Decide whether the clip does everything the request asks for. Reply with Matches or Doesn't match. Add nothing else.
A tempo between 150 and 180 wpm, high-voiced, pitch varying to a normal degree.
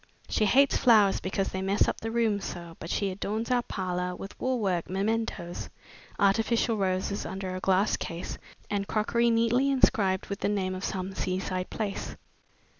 Matches